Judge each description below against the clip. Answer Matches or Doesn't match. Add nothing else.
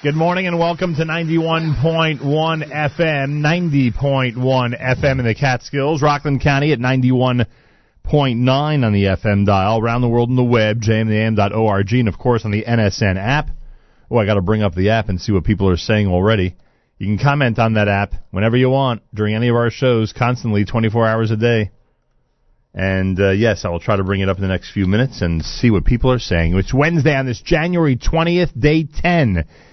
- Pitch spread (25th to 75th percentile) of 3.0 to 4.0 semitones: Doesn't match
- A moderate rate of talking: Matches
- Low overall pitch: Matches